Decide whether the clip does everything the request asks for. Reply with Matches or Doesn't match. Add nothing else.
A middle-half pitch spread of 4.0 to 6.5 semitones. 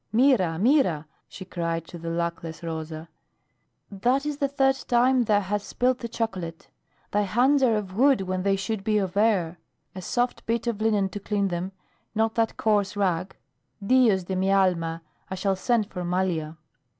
Matches